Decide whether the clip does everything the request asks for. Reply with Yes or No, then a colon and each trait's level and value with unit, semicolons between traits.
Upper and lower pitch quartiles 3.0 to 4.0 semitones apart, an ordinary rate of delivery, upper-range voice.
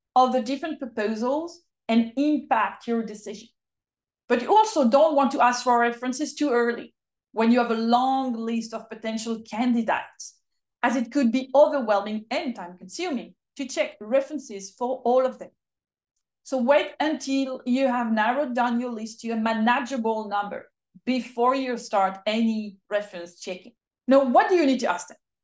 Yes: average, 3.3 semitones; average, 165 wpm; high, 245 Hz